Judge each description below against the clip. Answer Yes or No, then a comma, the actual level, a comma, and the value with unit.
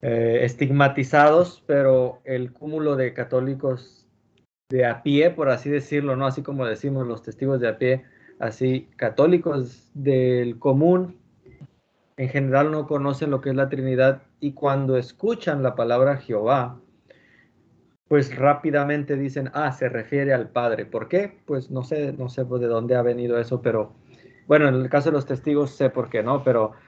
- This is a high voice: No, low, 135 Hz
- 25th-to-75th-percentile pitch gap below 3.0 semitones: Yes, narrow, 2.4 semitones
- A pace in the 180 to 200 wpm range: No, average, 165 wpm